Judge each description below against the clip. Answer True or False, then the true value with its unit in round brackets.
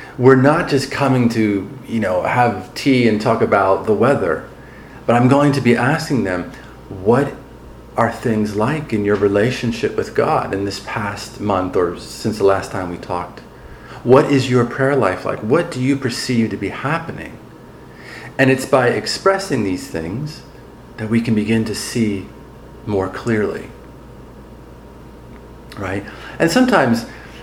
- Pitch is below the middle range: True (115 Hz)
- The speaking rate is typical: True (155 wpm)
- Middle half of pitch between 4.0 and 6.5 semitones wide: True (4.6 semitones)